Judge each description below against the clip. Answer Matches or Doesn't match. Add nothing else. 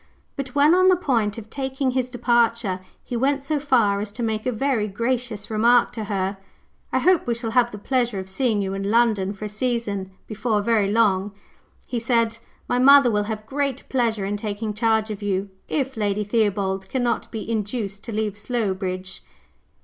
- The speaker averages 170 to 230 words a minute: Matches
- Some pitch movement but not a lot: Matches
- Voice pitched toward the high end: Matches